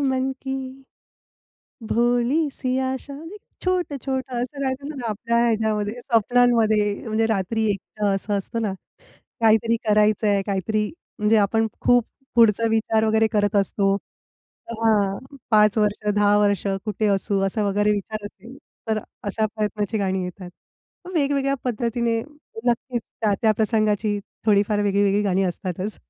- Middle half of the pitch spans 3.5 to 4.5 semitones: No, average, 2.9 semitones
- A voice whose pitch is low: No, high, 220 Hz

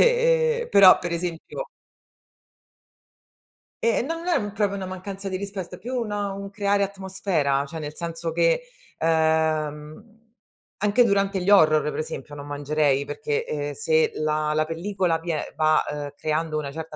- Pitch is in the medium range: Yes, medium, 170 Hz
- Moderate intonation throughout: Yes, average, 4.7 semitones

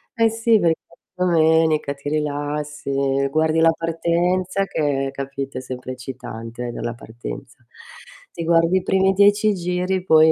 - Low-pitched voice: No, medium, 160 Hz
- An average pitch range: Yes, average, 4.7 semitones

